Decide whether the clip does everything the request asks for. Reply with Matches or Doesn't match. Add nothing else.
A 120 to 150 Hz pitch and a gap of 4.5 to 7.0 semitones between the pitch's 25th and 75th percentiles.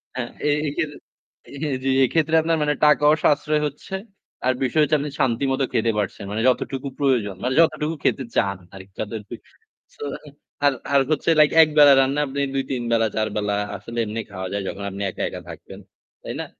Matches